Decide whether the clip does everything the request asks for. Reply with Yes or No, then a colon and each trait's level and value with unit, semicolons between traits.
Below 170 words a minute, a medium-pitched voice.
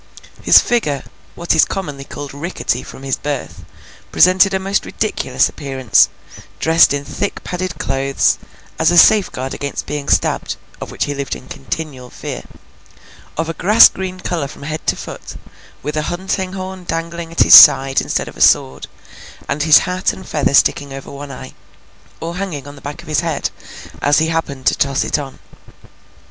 No: average, 175 wpm; medium, 150 Hz